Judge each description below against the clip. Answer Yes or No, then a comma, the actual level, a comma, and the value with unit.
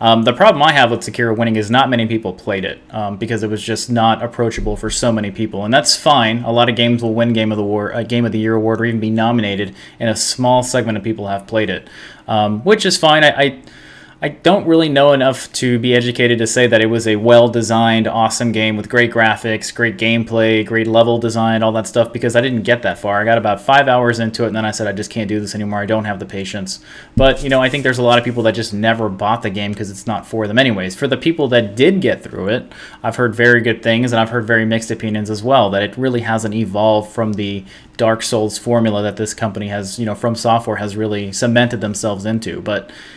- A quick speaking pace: Yes, fast, 260 wpm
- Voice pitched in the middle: No, low, 115 Hz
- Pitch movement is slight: Yes, narrow, 1.8 semitones